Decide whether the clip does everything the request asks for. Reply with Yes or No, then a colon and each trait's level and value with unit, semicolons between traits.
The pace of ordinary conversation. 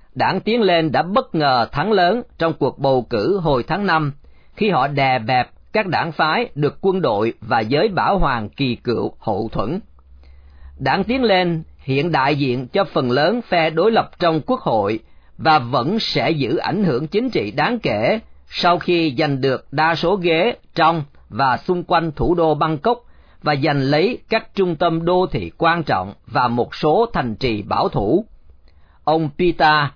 Yes: average, 180 wpm